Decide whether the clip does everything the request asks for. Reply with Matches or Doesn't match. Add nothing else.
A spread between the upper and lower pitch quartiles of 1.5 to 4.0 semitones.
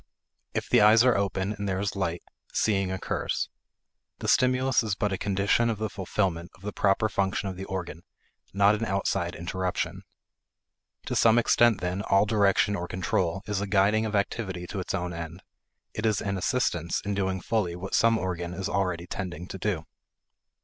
Matches